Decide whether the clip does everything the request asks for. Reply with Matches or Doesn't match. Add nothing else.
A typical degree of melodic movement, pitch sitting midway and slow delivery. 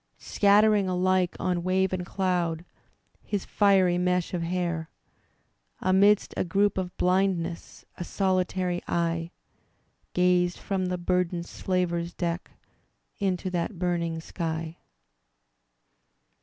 Doesn't match